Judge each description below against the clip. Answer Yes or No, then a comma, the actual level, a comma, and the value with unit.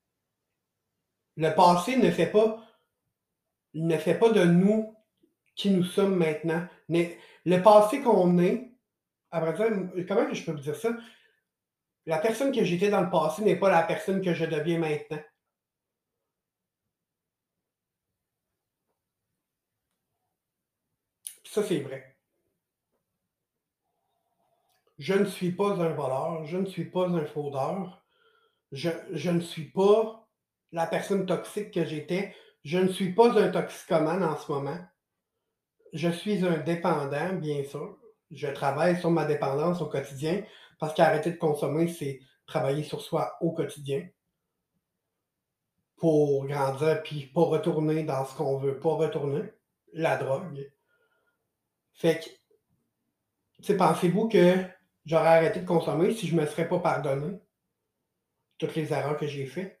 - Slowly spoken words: Yes, slow, 135 wpm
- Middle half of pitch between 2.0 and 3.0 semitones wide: No, average, 4.0 semitones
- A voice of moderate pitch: Yes, medium, 170 Hz